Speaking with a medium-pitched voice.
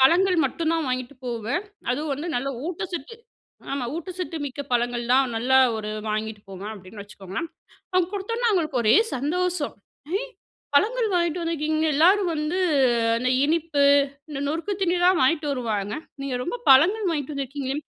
No: very high, 295 Hz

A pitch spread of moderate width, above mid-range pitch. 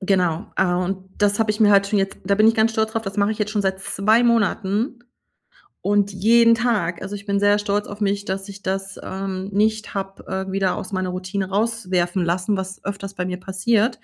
No: narrow, 2.0 semitones; high, 200 Hz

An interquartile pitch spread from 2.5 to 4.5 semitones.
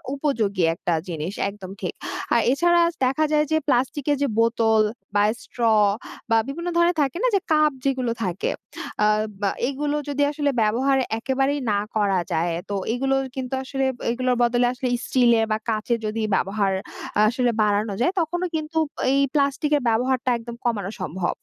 No: average, 4.9 semitones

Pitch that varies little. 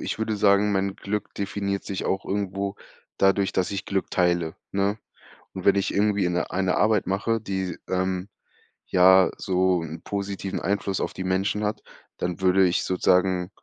Yes: narrow, 1.3 semitones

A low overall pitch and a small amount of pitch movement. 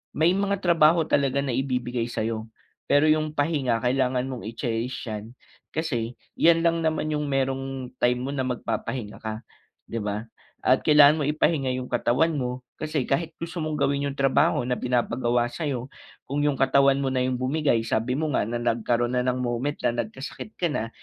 No: low, 130 Hz; average, 3.7 semitones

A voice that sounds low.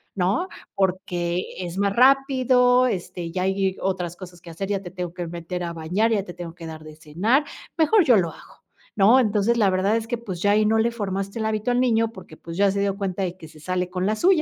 No: high, 195 Hz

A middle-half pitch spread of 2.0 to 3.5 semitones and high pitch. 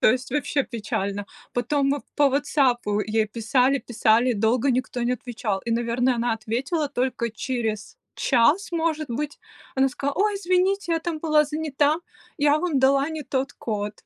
No: average, 4.3 semitones; very high, 260 Hz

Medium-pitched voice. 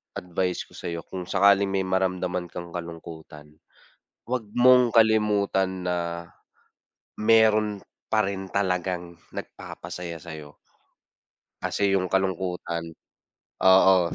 No: very low, 95 Hz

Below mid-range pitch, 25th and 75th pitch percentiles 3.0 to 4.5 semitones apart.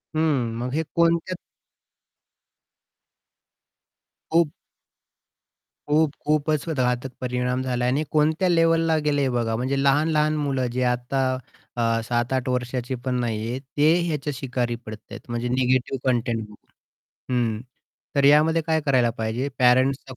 Yes: low, 130 Hz; average, 3.6 semitones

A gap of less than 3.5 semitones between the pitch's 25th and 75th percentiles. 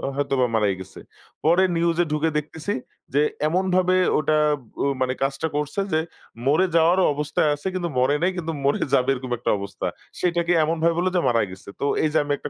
No: average, 3.9 semitones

